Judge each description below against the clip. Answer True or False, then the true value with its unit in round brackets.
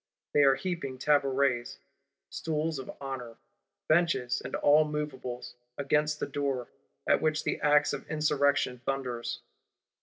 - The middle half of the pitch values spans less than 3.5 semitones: True (2.6 semitones)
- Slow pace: True (125 wpm)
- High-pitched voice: False (140 Hz)